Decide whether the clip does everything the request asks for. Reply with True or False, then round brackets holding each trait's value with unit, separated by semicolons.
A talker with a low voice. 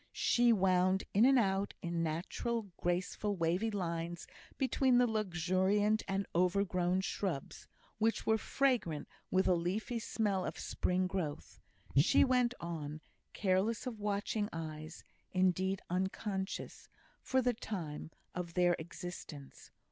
False (190 Hz)